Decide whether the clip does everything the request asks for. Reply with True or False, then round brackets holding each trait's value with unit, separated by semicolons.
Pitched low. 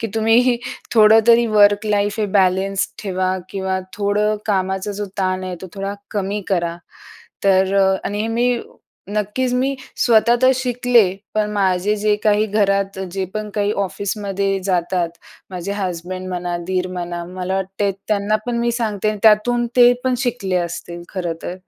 False (200 Hz)